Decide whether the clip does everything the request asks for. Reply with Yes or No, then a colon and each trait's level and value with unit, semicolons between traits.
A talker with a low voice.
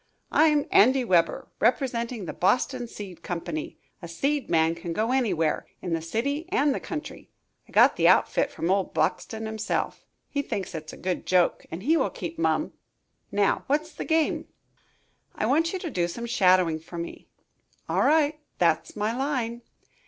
No: high, 220 Hz